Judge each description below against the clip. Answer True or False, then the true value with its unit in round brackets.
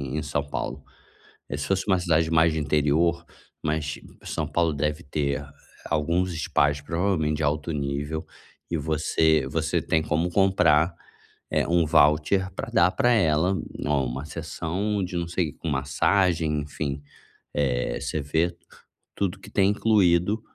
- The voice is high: False (80 Hz)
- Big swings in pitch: False (3.0 semitones)